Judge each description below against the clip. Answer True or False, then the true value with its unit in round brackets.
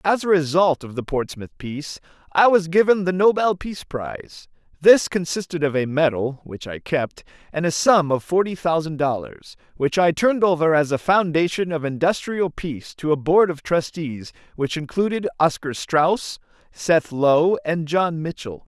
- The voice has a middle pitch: True (165 Hz)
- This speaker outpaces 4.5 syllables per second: True (4.7 syllables/s)